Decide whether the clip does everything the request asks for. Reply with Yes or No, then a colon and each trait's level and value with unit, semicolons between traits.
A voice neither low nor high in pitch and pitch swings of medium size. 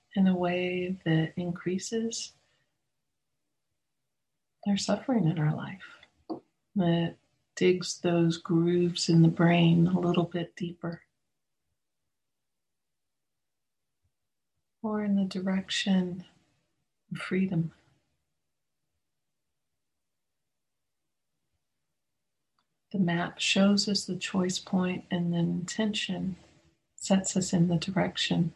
No: medium, 180 Hz; narrow, 2.0 semitones